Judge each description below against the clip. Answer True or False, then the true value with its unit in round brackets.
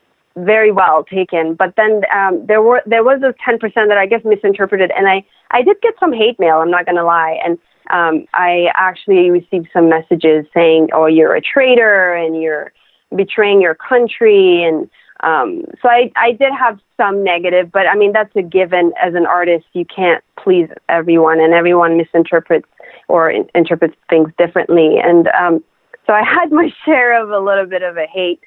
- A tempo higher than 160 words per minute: True (190 wpm)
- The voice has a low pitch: False (185 Hz)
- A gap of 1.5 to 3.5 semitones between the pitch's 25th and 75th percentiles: False (4.4 semitones)